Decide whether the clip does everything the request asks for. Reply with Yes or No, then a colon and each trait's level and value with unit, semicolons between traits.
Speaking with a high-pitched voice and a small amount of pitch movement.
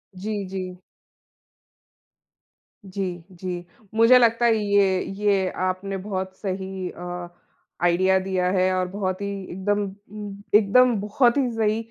Yes: high, 195 Hz; narrow, 2.0 semitones